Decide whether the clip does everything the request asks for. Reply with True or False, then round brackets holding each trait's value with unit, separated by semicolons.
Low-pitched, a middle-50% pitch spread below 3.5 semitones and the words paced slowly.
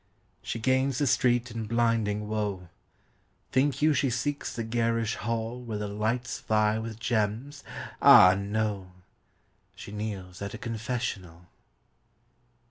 True (110 Hz; 2.7 semitones; 130 wpm)